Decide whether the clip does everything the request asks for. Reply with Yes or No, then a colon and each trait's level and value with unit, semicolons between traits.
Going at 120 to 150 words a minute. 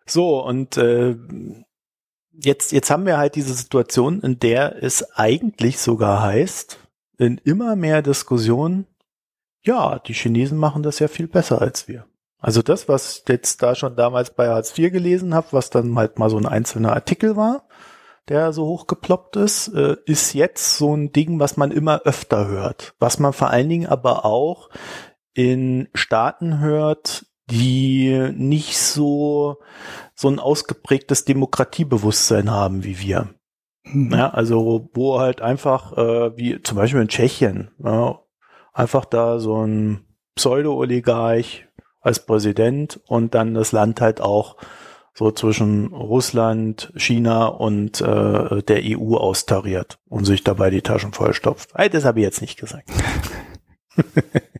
Yes: average, 145 wpm